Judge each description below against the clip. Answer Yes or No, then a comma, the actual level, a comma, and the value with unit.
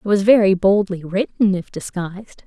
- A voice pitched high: Yes, high, 195 Hz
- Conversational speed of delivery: Yes, average, 170 wpm